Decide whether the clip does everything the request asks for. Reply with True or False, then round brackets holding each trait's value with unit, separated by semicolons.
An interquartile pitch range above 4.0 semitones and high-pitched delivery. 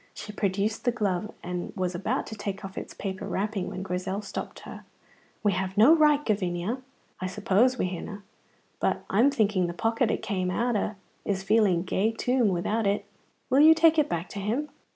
False (3.5 semitones; 205 Hz)